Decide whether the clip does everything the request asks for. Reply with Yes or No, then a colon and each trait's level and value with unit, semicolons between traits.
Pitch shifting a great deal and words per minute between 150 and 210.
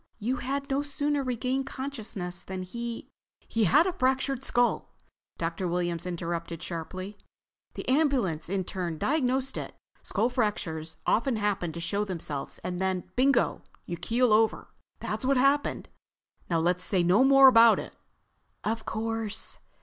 No: wide, 6.7 semitones; average, 140 wpm